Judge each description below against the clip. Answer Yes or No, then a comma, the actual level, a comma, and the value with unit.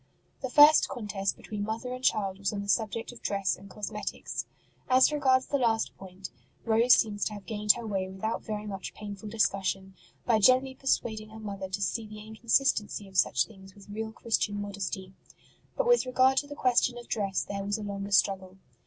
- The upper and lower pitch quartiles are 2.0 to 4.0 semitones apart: Yes, average, 3.2 semitones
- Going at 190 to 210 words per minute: Yes, average, 195 wpm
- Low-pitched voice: No, high, 210 Hz